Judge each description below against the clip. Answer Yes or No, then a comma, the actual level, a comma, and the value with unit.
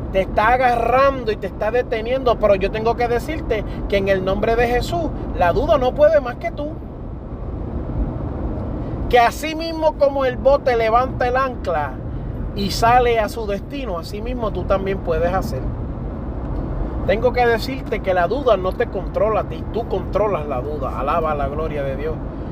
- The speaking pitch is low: No, high, 240 Hz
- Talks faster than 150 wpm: Yes, average, 170 wpm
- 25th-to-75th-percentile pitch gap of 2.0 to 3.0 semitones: No, average, 3.4 semitones